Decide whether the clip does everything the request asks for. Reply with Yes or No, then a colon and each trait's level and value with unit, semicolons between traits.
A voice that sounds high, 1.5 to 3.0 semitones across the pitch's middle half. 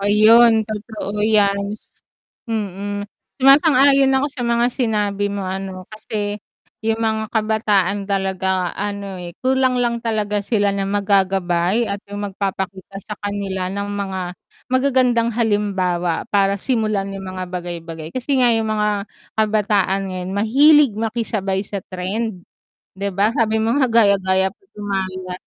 Yes: high, 205 Hz; narrow, 2.6 semitones